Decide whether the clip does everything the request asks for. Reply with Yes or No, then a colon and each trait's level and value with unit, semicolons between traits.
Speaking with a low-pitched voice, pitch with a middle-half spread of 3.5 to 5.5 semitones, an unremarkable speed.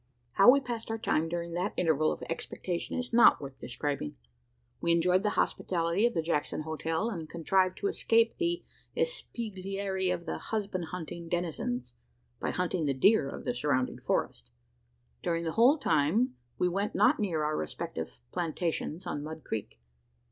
No: medium, 175 Hz; average, 4.8 semitones; average, 160 wpm